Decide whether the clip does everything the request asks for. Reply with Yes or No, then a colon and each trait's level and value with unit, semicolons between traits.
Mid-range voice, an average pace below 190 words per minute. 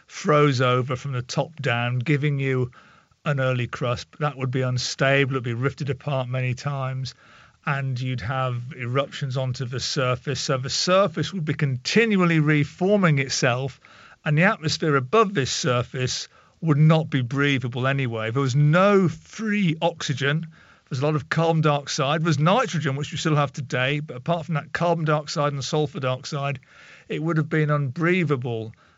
Yes: medium, 145 Hz; average, 165 wpm